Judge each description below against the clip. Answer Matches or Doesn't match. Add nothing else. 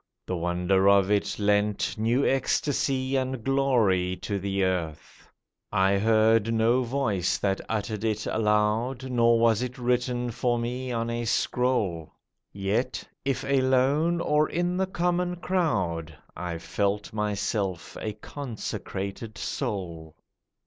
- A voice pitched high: Doesn't match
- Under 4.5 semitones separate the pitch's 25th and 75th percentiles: Doesn't match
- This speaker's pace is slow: Matches